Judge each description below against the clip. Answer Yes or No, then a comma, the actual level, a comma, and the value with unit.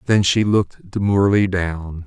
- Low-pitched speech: Yes, very low, 95 Hz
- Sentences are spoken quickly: No, average, 145 wpm